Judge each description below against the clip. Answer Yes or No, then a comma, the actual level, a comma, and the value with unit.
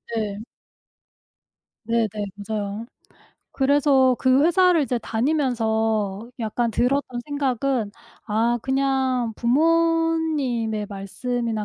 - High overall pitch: Yes, high, 245 Hz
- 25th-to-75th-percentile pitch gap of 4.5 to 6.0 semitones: No, average, 4.0 semitones